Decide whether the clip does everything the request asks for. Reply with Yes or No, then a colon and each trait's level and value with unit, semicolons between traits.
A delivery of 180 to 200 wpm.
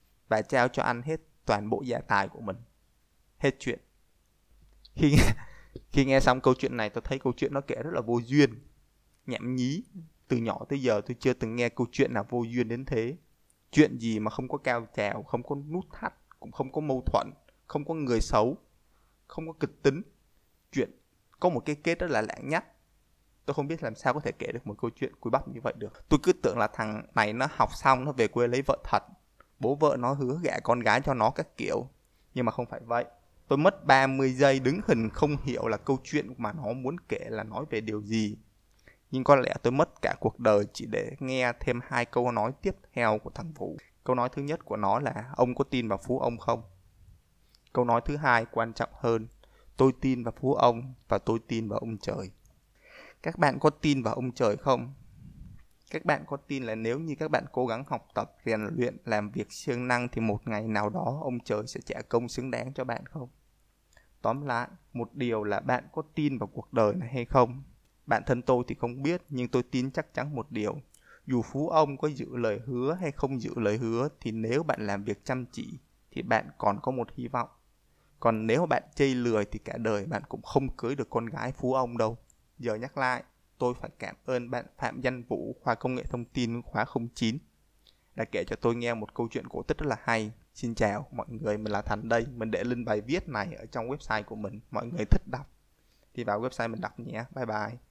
No: average, 230 wpm